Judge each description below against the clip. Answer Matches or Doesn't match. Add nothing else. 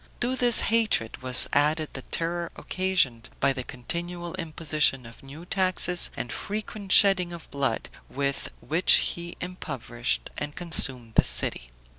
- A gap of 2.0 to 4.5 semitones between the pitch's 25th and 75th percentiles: Doesn't match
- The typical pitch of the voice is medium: Matches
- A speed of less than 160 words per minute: Matches